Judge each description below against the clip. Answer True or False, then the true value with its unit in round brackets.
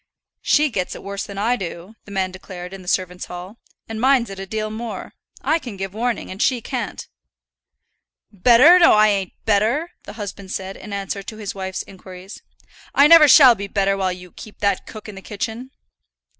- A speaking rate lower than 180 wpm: False (200 wpm)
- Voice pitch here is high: True (200 Hz)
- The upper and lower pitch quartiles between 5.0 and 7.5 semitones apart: False (3.4 semitones)